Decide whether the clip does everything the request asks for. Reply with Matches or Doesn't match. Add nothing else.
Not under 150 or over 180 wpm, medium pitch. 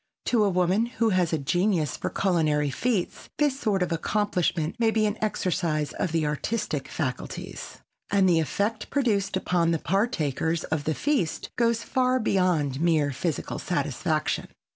Matches